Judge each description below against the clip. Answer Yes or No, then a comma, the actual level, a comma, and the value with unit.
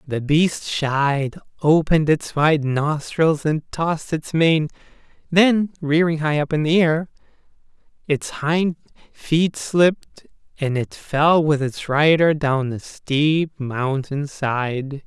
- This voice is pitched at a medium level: Yes, medium, 150 Hz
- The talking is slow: Yes, slow, 130 wpm